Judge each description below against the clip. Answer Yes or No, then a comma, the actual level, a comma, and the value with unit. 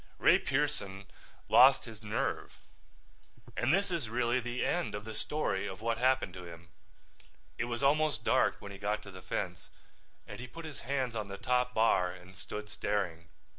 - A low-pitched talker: Yes, low, 115 Hz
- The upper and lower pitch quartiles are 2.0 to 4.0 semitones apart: No, average, 4.5 semitones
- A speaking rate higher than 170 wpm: Yes, average, 180 wpm